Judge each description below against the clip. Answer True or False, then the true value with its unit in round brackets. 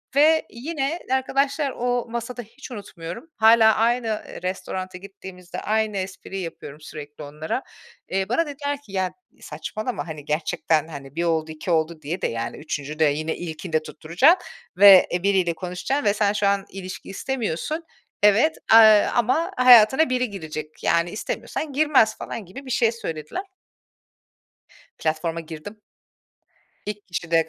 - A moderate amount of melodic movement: False (6.9 semitones)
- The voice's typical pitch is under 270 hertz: True (195 Hz)